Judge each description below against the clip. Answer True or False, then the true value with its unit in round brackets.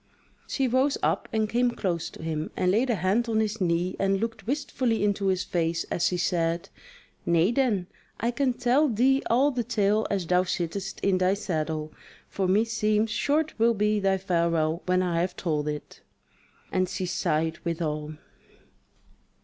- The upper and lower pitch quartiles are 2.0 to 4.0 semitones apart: False (5.0 semitones)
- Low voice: False (195 Hz)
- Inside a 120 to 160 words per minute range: False (170 wpm)